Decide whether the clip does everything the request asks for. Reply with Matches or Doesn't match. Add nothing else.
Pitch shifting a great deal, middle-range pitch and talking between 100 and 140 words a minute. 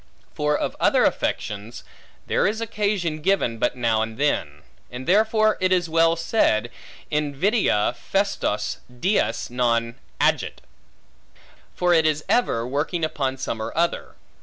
Matches